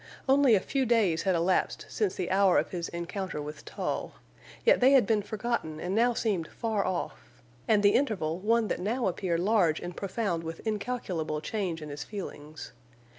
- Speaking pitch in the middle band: No, high, 195 Hz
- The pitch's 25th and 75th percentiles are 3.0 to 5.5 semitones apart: Yes, average, 5.1 semitones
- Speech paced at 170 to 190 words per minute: Yes, average, 180 wpm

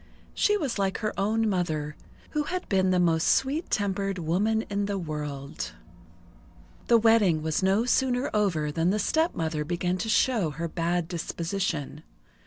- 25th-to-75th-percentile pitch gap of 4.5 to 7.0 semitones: Yes, average, 5.1 semitones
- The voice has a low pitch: No, high, 190 Hz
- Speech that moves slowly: No, average, 155 wpm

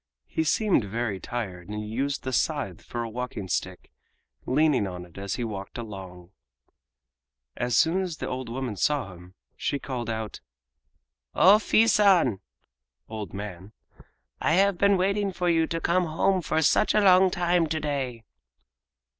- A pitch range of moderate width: No, wide, 8.7 semitones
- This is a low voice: Yes, low, 130 Hz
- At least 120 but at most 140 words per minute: No, average, 160 wpm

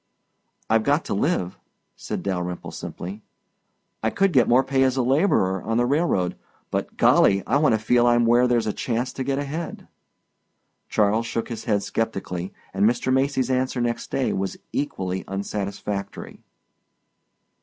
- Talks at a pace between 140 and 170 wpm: Yes, average, 155 wpm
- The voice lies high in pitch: No, low, 115 Hz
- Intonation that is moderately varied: Yes, average, 4.9 semitones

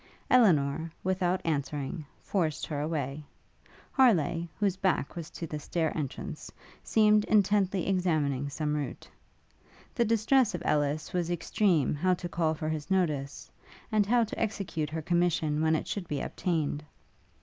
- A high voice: No, medium, 165 Hz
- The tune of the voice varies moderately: Yes, average, 4.2 semitones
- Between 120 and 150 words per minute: Yes, average, 145 wpm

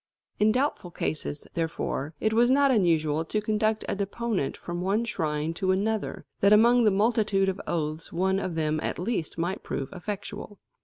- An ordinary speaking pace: Yes, average, 170 wpm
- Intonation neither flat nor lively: Yes, average, 4.7 semitones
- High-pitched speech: Yes, high, 195 Hz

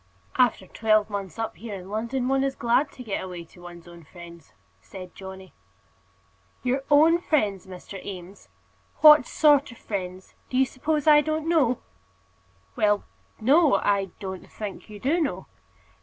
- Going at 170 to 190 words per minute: No, average, 155 wpm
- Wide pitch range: Yes, wide, 6.3 semitones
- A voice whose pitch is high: Yes, high, 215 Hz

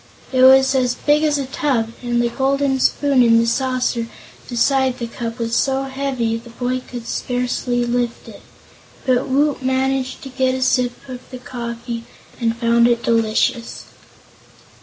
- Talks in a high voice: Yes, very high, 250 Hz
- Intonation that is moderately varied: No, narrow, 2.1 semitones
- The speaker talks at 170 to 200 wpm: No, average, 160 wpm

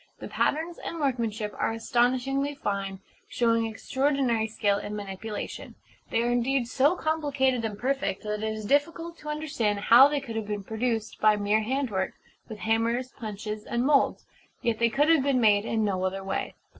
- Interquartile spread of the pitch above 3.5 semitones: Yes, average, 4.4 semitones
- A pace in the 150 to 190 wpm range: Yes, average, 175 wpm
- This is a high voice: Yes, high, 230 Hz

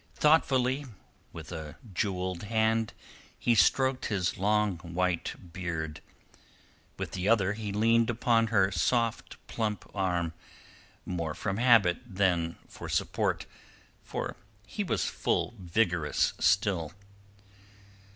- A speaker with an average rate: No, slow, 110 wpm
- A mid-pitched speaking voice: No, low, 100 Hz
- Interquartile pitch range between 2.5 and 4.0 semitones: No, average, 4.5 semitones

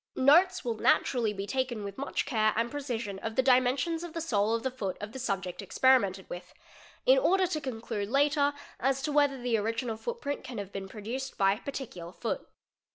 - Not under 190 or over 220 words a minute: Yes, fast, 205 wpm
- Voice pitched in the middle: No, high, 245 Hz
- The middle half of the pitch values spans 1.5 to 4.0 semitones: No, average, 5.0 semitones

